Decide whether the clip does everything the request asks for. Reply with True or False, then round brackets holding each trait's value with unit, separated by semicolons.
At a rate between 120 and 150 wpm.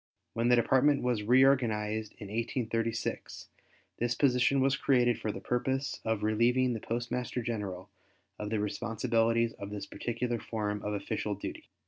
True (145 wpm)